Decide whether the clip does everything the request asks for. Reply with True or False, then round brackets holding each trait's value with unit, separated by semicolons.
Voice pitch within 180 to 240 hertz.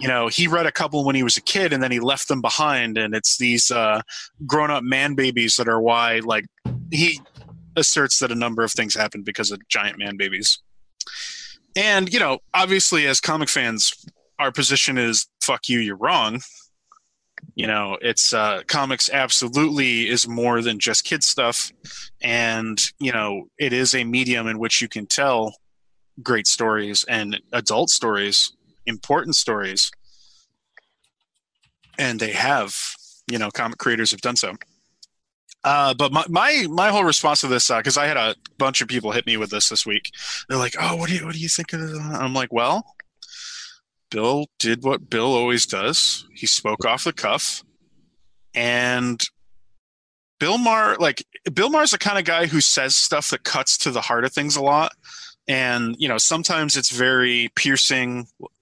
False (125 Hz)